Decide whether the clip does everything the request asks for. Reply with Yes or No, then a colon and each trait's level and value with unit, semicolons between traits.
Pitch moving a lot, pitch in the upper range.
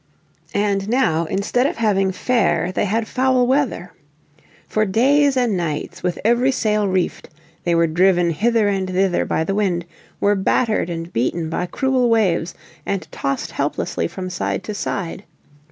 No: average, 4.7 semitones; high, 195 Hz